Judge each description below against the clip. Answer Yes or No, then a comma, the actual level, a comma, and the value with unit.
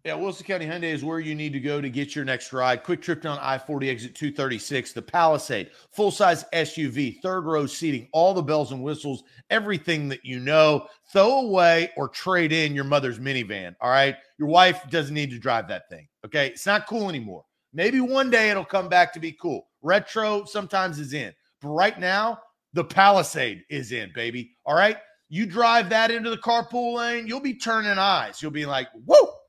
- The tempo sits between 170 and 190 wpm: No, fast, 205 wpm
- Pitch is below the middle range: No, medium, 165 Hz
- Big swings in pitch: Yes, wide, 6.3 semitones